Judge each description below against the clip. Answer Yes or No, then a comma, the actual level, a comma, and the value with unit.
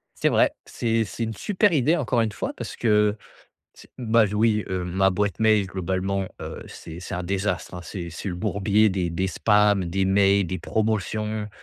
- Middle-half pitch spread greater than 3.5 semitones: No, narrow, 2.6 semitones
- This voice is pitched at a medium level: No, low, 100 Hz